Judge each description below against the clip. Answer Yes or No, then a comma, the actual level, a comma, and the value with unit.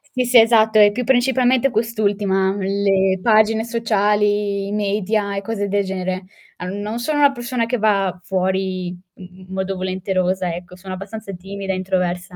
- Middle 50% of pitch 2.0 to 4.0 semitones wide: Yes, average, 2.7 semitones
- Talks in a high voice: Yes, high, 200 Hz